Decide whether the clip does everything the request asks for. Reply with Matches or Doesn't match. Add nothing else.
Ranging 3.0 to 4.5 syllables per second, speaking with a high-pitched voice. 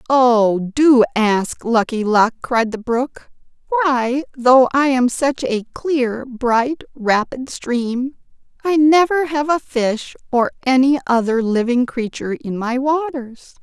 Matches